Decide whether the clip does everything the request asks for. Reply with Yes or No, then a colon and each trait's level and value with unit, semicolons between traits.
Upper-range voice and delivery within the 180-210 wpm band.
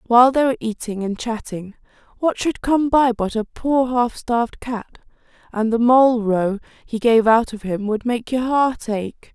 Yes: high, 235 Hz; average, 195 wpm